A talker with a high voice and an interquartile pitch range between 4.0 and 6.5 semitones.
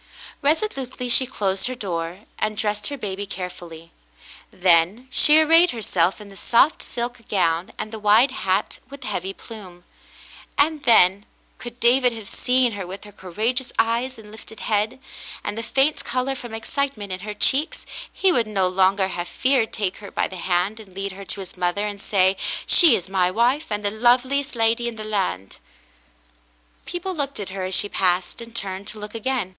Yes: high, 215 Hz; average, 4.8 semitones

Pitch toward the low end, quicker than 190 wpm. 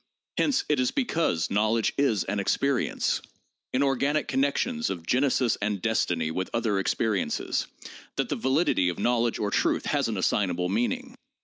No: low, 115 Hz; average, 150 wpm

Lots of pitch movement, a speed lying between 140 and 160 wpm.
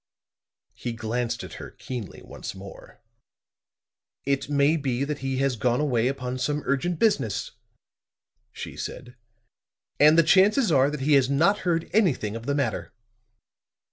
No: average, 3.7 semitones; average, 145 wpm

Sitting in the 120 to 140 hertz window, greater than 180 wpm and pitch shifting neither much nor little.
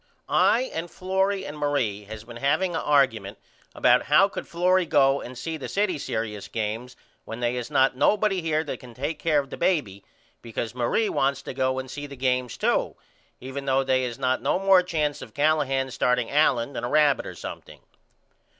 Yes: low, 135 Hz; average, 195 wpm; average, 4.0 semitones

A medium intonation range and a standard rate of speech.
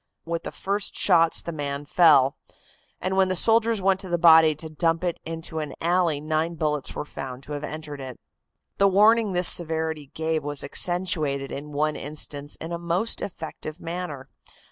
Yes: average, 3.1 semitones; average, 180 wpm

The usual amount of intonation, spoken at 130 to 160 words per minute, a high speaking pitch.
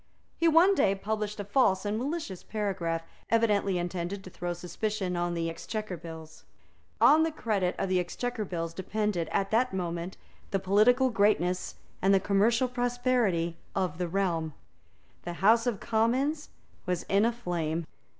Yes: average, 4.6 semitones; average, 155 wpm; high, 195 Hz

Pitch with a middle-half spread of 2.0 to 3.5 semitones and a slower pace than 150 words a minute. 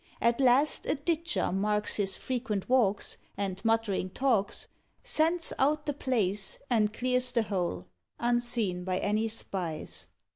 No: average, 4.6 semitones; slow, 135 wpm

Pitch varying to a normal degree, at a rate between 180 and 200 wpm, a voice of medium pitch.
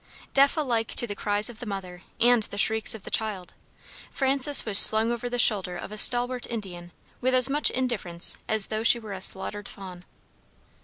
No: average, 3.6 semitones; average, 195 wpm; high, 220 Hz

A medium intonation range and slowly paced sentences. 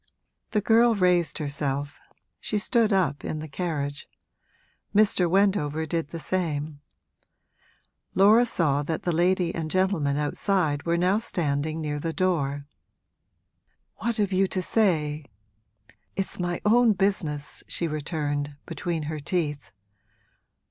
Yes: average, 4.4 semitones; slow, 125 wpm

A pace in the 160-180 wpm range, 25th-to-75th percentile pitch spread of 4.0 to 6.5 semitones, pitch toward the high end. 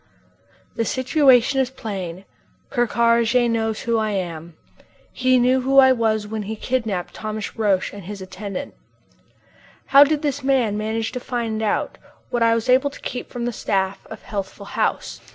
No: average, 170 wpm; average, 3.6 semitones; high, 230 Hz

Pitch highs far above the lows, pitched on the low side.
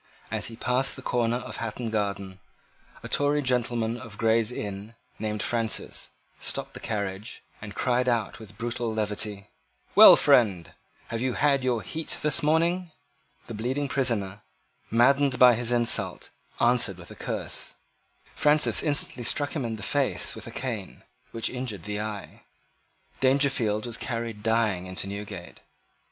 No: average, 3.4 semitones; low, 115 Hz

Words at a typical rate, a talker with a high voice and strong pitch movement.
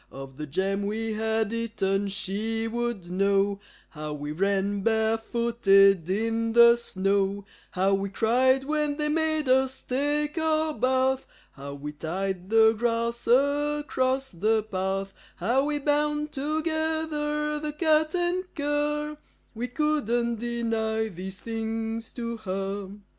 No: slow, 125 wpm; high, 230 Hz; wide, 6.7 semitones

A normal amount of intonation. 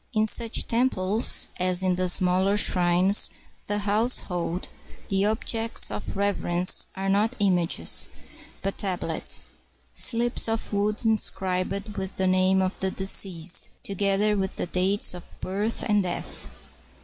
No: narrow, 2.3 semitones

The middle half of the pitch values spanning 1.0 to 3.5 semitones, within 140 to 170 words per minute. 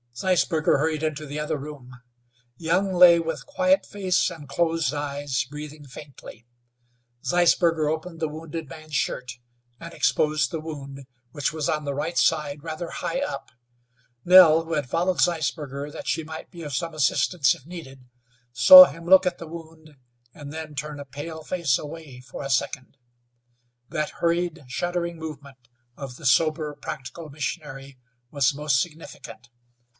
Yes: average, 2.9 semitones; average, 155 wpm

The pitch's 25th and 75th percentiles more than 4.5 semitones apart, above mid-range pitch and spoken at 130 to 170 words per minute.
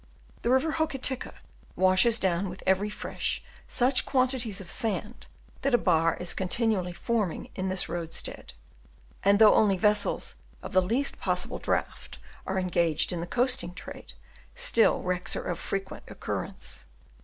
Yes: average, 4.9 semitones; high, 195 Hz; average, 145 wpm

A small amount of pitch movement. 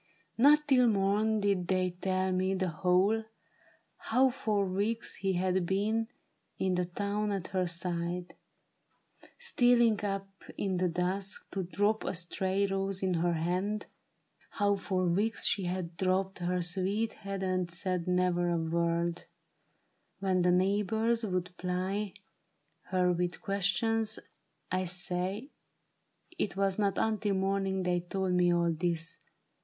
Yes: narrow, 2.2 semitones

